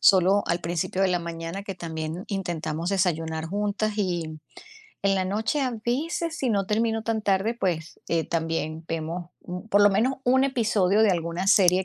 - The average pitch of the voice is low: No, high, 190 Hz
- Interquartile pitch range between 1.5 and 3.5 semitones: No, average, 4.3 semitones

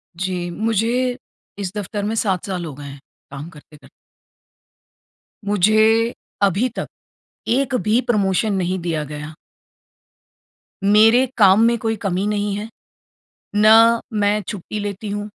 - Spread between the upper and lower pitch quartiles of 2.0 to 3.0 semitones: No, average, 3.5 semitones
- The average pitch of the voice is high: Yes, high, 205 Hz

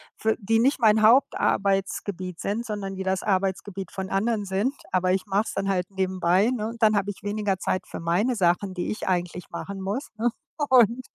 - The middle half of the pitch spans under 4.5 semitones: Yes, narrow, 2.6 semitones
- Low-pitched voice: No, high, 195 Hz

